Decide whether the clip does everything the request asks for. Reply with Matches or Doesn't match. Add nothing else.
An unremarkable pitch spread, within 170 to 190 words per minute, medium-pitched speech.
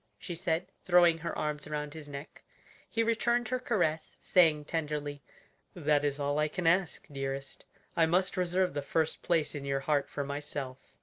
Matches